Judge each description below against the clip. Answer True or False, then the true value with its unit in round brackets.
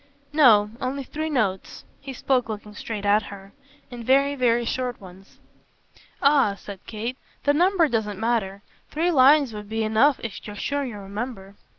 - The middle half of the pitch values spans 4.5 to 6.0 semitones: True (4.9 semitones)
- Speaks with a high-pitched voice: True (230 Hz)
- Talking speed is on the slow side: False (165 wpm)